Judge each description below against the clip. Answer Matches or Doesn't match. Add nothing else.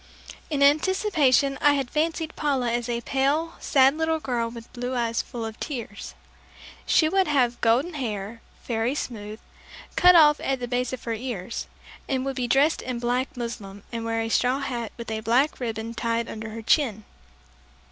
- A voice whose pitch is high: Matches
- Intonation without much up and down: Doesn't match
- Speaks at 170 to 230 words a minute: Matches